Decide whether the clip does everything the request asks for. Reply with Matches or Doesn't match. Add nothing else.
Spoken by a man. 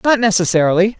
Doesn't match